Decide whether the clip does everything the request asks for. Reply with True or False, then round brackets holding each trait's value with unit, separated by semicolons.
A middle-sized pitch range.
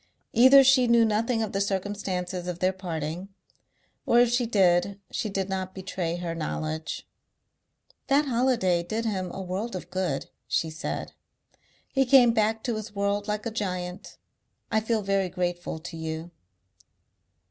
True (4.0 semitones)